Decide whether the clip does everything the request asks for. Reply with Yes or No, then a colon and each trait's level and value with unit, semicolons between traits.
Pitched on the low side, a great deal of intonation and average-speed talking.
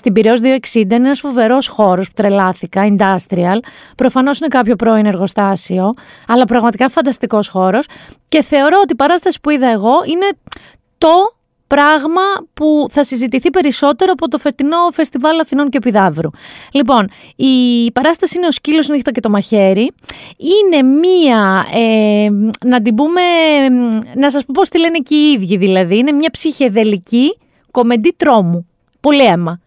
No: very high, 260 Hz; wide, 5.9 semitones; average, 150 wpm